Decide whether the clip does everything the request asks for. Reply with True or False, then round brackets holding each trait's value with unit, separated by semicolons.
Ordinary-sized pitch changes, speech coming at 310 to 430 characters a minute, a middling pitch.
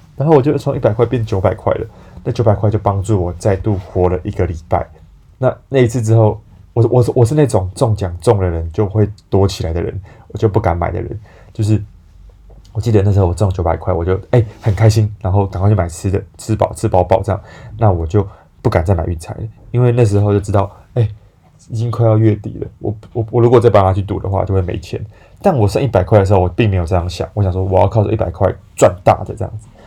False (3.1 semitones; 340 characters per minute; 105 Hz)